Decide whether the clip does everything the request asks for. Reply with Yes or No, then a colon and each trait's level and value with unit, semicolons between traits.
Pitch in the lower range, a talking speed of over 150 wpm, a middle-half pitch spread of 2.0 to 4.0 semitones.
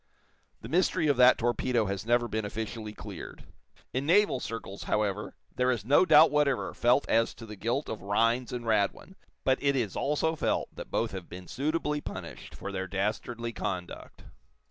No: low, 120 Hz; average, 175 wpm; average, 4.8 semitones